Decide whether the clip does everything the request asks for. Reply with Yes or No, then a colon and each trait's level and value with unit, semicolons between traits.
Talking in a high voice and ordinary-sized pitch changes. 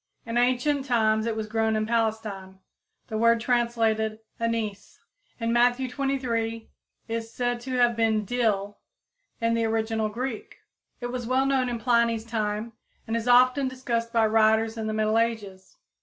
No: high, 230 Hz; narrow, 1.8 semitones